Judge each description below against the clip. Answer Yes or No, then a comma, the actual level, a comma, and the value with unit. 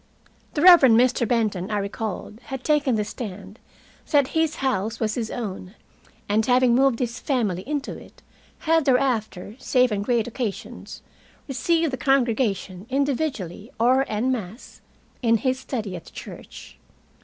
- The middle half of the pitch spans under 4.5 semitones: Yes, average, 4.0 semitones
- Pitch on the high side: Yes, high, 240 Hz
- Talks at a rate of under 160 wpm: Yes, average, 145 wpm